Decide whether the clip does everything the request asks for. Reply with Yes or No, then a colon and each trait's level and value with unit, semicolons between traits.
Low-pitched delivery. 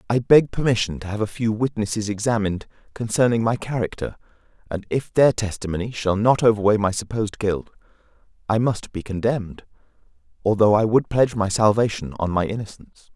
Yes: low, 110 Hz